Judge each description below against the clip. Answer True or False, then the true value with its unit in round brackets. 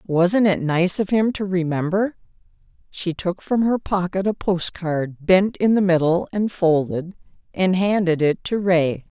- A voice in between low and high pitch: True (180 Hz)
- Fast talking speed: False (165 wpm)